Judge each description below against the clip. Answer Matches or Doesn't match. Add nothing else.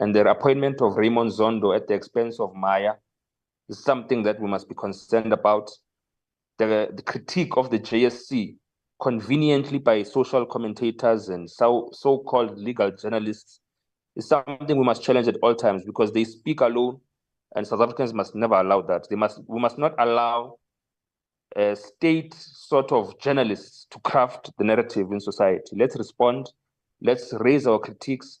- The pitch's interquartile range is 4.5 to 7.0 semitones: Doesn't match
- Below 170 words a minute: Matches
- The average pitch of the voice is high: Doesn't match